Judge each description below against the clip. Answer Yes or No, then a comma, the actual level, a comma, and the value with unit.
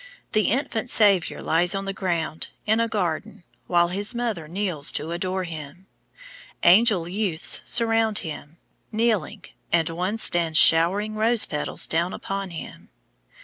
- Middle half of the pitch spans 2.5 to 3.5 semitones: No, average, 4.4 semitones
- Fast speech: No, average, 140 wpm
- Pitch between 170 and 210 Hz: Yes, high, 190 Hz